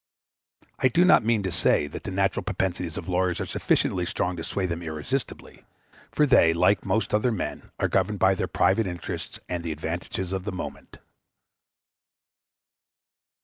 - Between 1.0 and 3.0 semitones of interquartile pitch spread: No, average, 3.9 semitones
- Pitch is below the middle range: Yes, very low, 90 Hz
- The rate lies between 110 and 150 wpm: No, average, 165 wpm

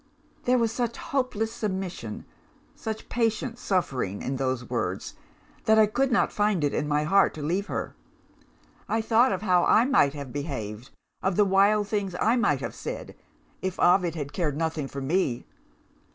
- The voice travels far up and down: Yes, wide, 7.1 semitones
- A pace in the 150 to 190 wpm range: Yes, average, 170 wpm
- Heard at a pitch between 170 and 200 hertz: Yes, high, 190 Hz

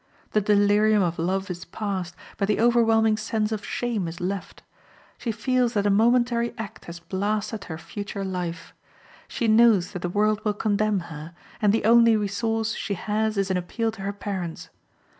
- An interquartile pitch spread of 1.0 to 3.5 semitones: Yes, average, 2.7 semitones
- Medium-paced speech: Yes, average, 180 wpm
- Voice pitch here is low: No, high, 210 Hz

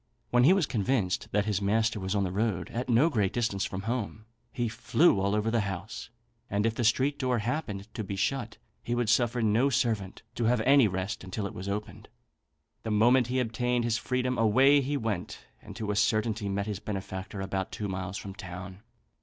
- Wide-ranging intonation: No, average, 3.5 semitones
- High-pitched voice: No, low, 110 Hz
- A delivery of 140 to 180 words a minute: No, fast, 205 wpm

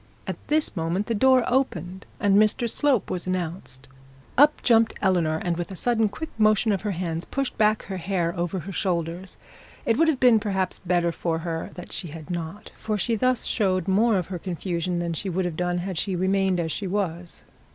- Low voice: No, medium, 185 Hz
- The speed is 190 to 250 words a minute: Yes, fast, 205 wpm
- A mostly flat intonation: No, average, 3.7 semitones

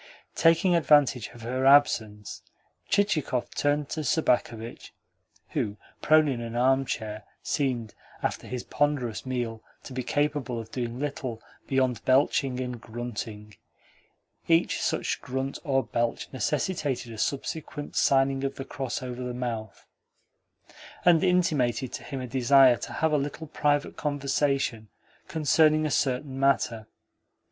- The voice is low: Yes, low, 130 Hz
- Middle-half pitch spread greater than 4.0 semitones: No, average, 3.4 semitones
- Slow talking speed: Yes, slow, 130 wpm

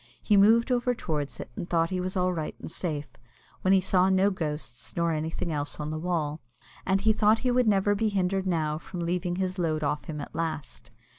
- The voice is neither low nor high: Yes, medium, 180 Hz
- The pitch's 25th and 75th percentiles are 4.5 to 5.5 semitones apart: No, average, 3.7 semitones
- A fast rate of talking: Yes, fast, 220 wpm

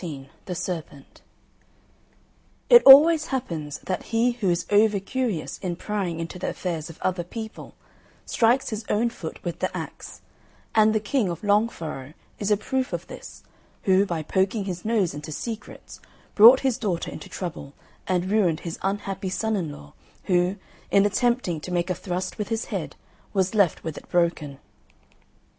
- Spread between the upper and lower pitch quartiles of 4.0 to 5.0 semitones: Yes, average, 4.3 semitones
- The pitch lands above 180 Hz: Yes, high, 190 Hz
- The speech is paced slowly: No, average, 170 wpm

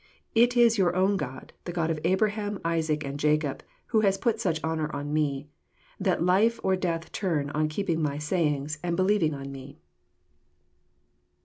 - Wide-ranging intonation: No, average, 4.3 semitones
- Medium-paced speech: Yes, average, 170 wpm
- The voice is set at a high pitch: No, medium, 165 Hz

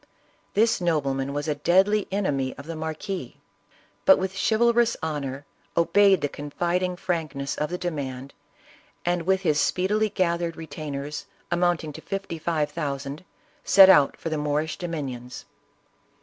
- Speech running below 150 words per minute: Yes, average, 140 wpm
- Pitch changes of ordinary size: Yes, average, 4.3 semitones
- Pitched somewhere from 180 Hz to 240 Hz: No, medium, 160 Hz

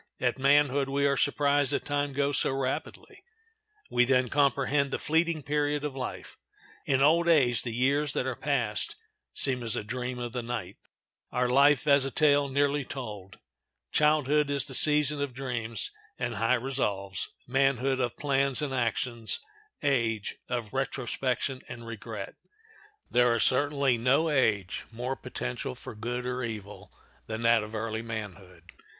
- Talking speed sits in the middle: Yes, average, 155 wpm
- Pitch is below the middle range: Yes, low, 130 Hz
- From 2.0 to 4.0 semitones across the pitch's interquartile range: Yes, average, 3.4 semitones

